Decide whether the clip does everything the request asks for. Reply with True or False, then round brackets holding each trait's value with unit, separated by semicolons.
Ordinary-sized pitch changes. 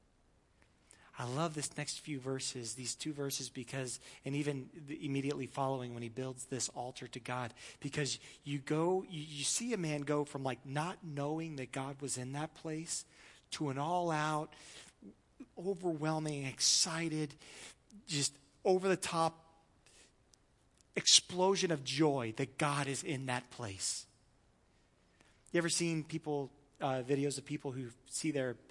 True (3.0 semitones)